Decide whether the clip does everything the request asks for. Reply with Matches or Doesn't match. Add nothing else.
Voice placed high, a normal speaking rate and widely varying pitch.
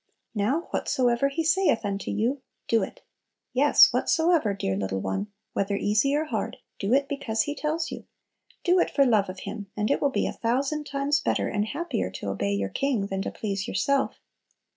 Matches